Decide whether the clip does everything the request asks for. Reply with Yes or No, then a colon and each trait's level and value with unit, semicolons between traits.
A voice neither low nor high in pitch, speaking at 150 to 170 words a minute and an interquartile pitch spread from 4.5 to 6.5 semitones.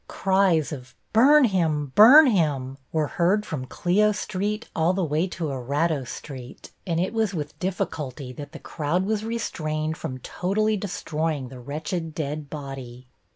Yes: medium, 160 Hz; average, 155 wpm; average, 5.2 semitones